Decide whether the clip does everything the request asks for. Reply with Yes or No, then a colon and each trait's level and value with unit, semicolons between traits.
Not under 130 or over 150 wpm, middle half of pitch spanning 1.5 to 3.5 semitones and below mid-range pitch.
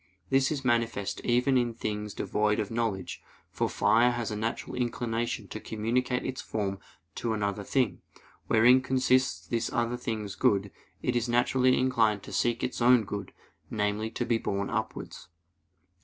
No: average, 160 wpm; average, 2.8 semitones; low, 115 Hz